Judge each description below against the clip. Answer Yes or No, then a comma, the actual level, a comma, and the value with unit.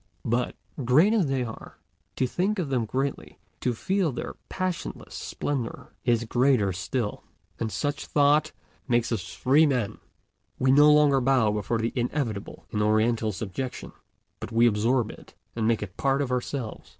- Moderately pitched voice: No, low, 125 Hz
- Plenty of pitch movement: No, average, 4.0 semitones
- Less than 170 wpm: Yes, average, 160 wpm